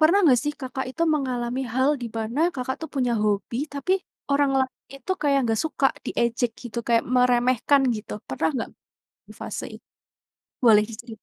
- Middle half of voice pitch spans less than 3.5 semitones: Yes, average, 2.9 semitones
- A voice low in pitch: No, very high, 250 Hz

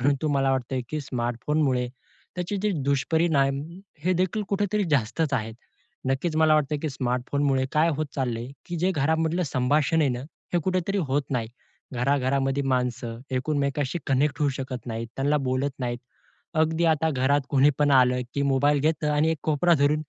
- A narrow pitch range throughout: No, average, 3.2 semitones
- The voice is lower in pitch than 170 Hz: Yes, medium, 140 Hz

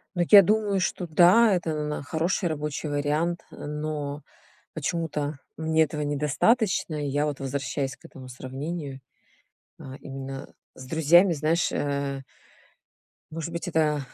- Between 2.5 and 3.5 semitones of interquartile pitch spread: Yes, average, 3.1 semitones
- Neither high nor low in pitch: Yes, medium, 150 Hz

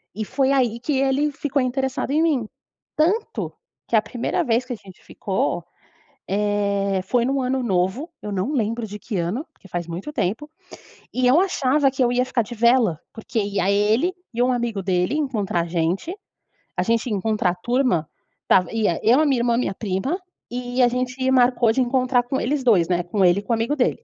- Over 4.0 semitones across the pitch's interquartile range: Yes, average, 4.6 semitones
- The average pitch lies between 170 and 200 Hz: No, high, 240 Hz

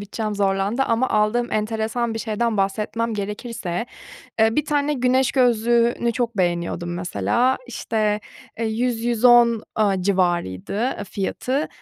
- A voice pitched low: No, high, 220 Hz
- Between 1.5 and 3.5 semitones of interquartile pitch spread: Yes, average, 3.2 semitones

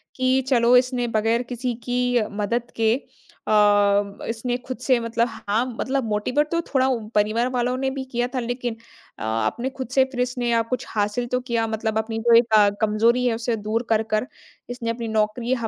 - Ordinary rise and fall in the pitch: No, narrow, 2.1 semitones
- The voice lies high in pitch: Yes, high, 235 Hz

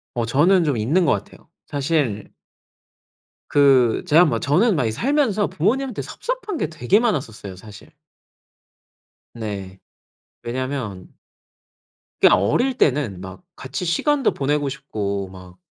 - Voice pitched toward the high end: No, medium, 140 Hz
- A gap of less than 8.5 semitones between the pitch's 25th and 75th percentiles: No, wide, 9.0 semitones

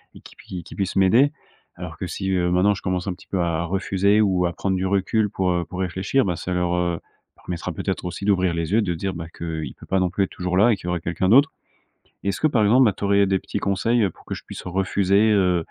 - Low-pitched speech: Yes, very low, 95 Hz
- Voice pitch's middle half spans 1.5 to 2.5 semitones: Yes, narrow, 2.1 semitones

